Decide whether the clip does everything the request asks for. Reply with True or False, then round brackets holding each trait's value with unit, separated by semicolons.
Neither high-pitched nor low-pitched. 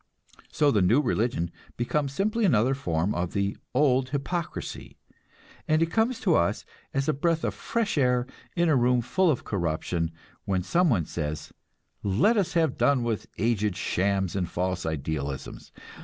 False (120 Hz)